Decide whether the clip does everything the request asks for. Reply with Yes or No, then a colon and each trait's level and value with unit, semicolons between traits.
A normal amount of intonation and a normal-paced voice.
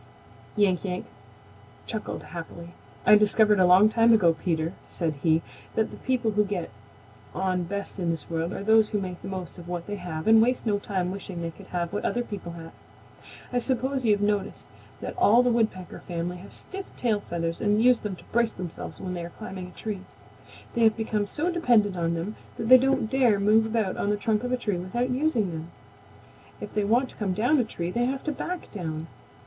No: average, 4.3 semitones; fast, 215 wpm